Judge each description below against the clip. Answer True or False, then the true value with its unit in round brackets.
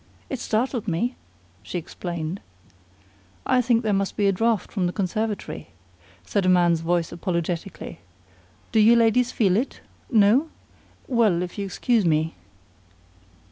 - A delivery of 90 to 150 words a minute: True (140 wpm)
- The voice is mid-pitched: False (200 Hz)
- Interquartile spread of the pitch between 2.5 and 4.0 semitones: False (4.7 semitones)